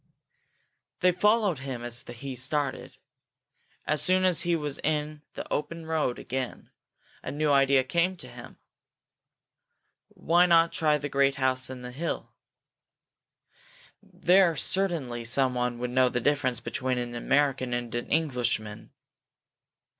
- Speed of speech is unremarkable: No, slow, 130 wpm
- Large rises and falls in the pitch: No, average, 4.8 semitones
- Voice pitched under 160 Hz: Yes, medium, 140 Hz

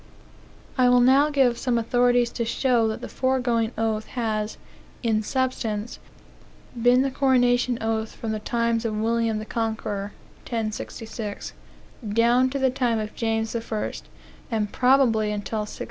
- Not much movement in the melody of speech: Yes, narrow, 2.2 semitones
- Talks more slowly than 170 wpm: Yes, average, 145 wpm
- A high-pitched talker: Yes, high, 230 Hz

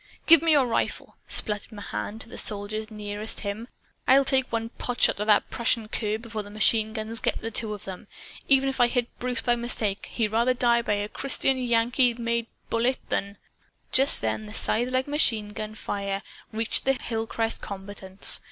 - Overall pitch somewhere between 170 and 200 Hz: No, high, 225 Hz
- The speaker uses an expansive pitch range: No, average, 2.8 semitones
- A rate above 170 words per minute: Yes, average, 185 wpm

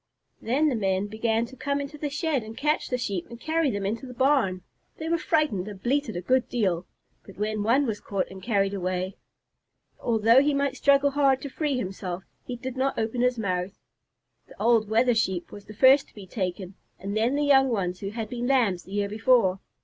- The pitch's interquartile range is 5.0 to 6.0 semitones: Yes, average, 5.3 semitones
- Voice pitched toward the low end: No, high, 230 Hz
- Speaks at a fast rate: Yes, fast, 215 wpm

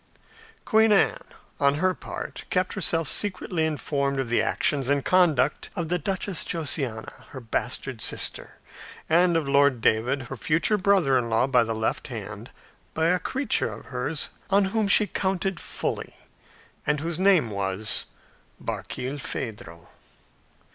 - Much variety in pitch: Yes, wide, 6.2 semitones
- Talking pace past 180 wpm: No, average, 140 wpm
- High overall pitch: No, medium, 150 Hz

